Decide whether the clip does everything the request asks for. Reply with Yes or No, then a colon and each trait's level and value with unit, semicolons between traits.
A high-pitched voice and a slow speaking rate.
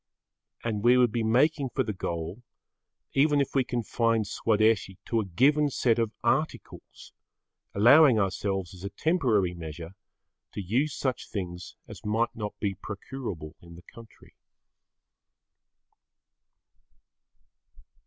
No: low, 110 Hz; slow, 125 wpm